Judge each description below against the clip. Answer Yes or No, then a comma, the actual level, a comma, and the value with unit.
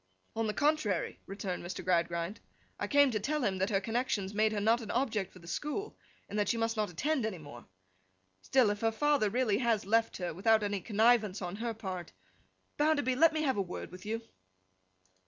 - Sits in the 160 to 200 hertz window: No, high, 215 Hz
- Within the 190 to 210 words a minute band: Yes, average, 200 wpm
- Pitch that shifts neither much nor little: Yes, average, 4.1 semitones